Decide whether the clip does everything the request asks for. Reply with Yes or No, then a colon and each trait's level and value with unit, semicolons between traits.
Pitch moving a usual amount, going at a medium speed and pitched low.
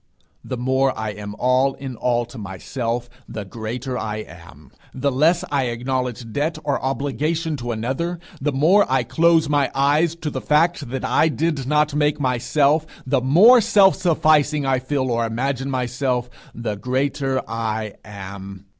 Yes: average, 4.1 semitones; average, 160 wpm; low, 130 Hz